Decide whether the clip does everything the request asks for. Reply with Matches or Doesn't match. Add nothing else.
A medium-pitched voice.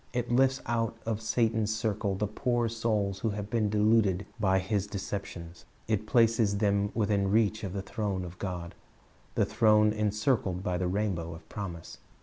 Doesn't match